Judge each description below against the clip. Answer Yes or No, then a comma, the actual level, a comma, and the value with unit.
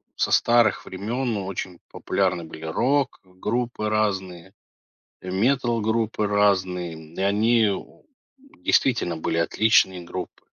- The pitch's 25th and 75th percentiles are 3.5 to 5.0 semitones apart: Yes, average, 3.9 semitones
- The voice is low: Yes, low, 100 Hz